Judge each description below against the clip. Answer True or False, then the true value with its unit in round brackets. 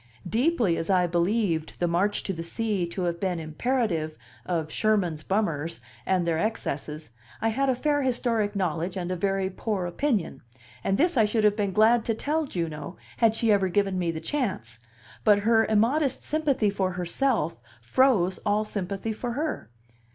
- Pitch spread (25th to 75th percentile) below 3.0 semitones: False (4.8 semitones)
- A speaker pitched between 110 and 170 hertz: False (200 Hz)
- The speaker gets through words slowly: False (175 wpm)